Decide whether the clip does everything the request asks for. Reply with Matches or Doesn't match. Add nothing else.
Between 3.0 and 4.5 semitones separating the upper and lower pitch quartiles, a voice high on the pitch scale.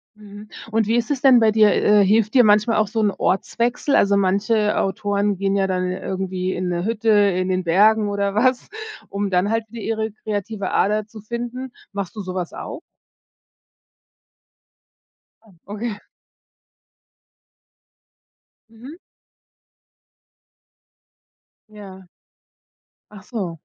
Doesn't match